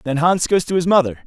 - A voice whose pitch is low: No, medium, 165 Hz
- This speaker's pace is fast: Yes, fast, 285 wpm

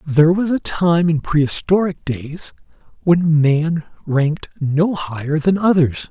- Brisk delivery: No, average, 140 wpm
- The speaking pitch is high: No, medium, 155 Hz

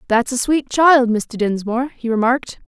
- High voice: Yes, high, 245 Hz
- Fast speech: No, average, 180 wpm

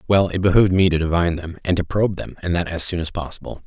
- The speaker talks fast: Yes, fast, 280 wpm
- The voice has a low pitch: Yes, very low, 90 Hz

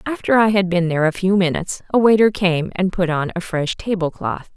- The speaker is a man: No, female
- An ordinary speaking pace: No, fast, 235 wpm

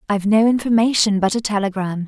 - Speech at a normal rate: Yes, average, 175 wpm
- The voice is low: No, high, 210 Hz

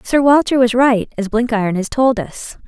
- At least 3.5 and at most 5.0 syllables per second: Yes, 4.8 syllables/s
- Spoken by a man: No, female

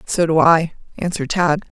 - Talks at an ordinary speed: Yes, average, 165 wpm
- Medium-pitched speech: Yes, medium, 165 Hz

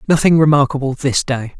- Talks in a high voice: No, medium, 140 Hz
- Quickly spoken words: No, average, 150 wpm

